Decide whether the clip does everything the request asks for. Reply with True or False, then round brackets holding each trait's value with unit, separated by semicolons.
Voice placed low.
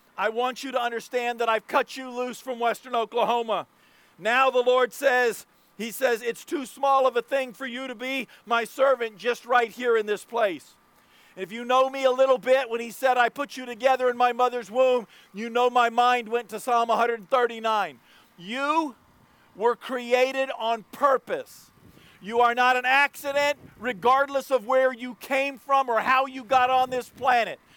False (250 Hz)